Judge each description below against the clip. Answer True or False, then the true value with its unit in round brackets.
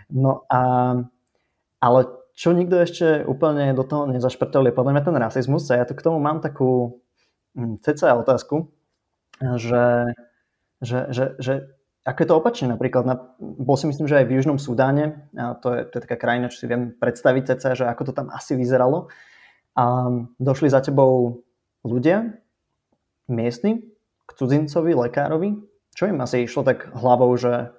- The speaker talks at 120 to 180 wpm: True (160 wpm)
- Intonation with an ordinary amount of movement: True (3.4 semitones)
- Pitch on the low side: True (130 Hz)